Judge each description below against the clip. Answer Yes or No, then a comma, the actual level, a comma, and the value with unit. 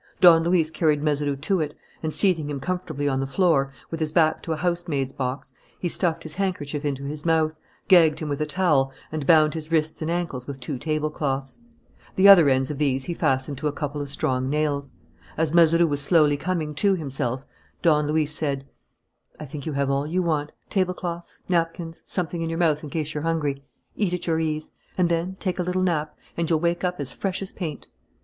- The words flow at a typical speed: No, fast, 210 wpm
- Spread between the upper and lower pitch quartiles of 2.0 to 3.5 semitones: Yes, average, 3.0 semitones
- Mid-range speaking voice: Yes, medium, 155 Hz